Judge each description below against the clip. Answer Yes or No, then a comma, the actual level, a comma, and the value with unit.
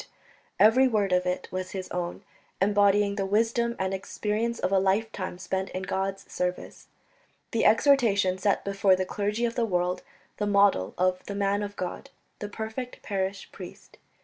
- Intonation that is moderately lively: No, narrow, 2.3 semitones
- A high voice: Yes, high, 200 Hz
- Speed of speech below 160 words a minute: No, average, 165 wpm